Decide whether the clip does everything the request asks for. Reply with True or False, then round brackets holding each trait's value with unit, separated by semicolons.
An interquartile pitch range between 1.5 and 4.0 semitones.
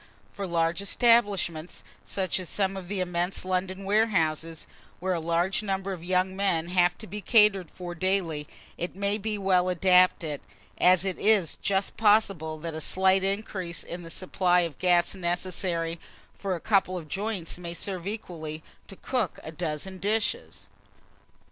True (2.5 semitones)